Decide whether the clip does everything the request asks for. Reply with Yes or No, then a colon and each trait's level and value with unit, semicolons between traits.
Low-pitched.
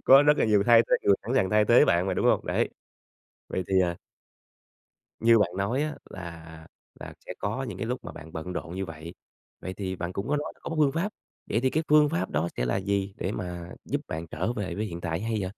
Yes: very low, 95 Hz